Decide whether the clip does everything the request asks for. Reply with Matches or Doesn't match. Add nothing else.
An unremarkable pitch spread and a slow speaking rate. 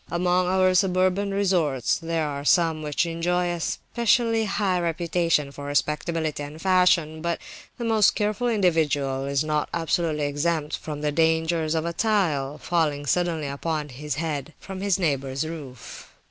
Doesn't match